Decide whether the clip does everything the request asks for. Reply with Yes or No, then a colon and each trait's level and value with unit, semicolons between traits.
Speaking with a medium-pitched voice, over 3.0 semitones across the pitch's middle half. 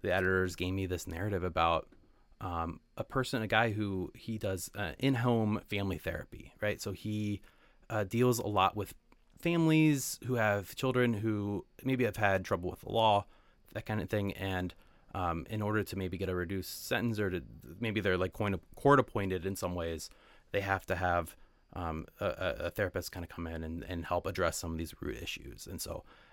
No: very low, 95 Hz; average, 3.5 semitones